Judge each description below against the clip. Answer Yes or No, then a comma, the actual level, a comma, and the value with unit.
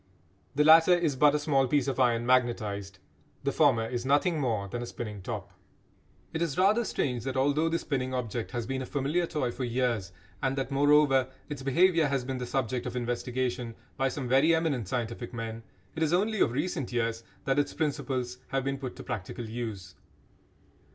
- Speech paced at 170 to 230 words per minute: Yes, average, 190 wpm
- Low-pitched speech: Yes, low, 130 Hz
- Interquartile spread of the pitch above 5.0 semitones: No, average, 3.4 semitones